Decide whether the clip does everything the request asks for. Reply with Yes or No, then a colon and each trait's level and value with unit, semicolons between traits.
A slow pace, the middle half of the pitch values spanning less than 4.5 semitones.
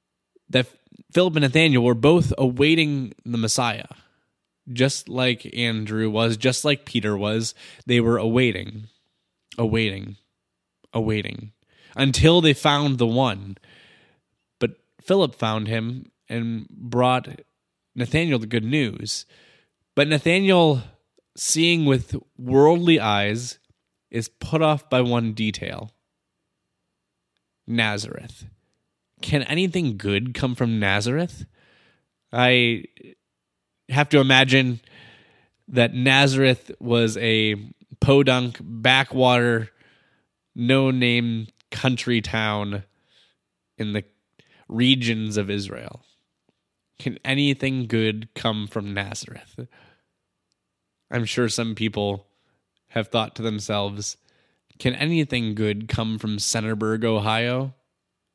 Yes: slow, 100 wpm; average, 3.7 semitones